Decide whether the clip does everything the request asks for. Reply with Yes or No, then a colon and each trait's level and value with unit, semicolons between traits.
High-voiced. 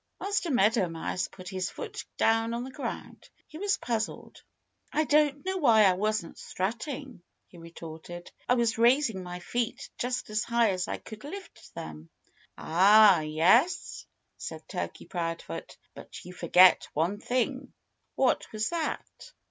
Yes: high, 220 Hz